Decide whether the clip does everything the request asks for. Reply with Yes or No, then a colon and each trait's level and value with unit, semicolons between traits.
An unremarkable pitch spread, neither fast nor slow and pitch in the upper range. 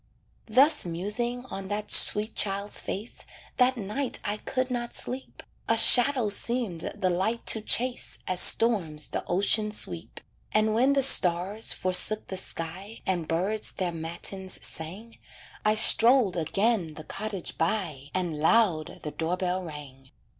Yes: average, 4.7 semitones; average, 145 wpm; high, 200 Hz